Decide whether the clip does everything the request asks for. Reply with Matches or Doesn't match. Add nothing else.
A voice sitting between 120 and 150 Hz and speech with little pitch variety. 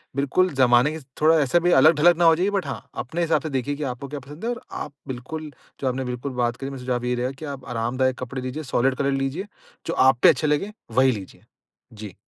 Doesn't match